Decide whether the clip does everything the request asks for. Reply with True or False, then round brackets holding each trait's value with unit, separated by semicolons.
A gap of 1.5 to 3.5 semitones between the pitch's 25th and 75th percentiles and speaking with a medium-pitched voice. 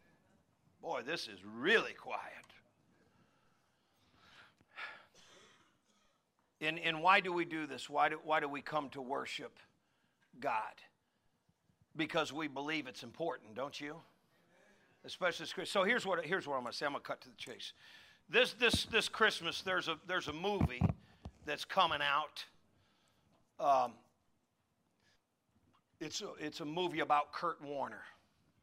True (3.0 semitones; 155 Hz)